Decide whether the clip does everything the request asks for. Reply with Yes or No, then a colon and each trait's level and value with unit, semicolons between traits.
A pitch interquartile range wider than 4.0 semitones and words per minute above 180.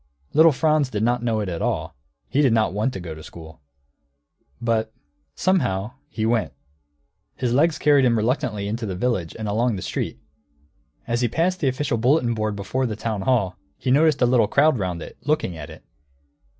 Yes: average, 4.4 semitones; average, 190 wpm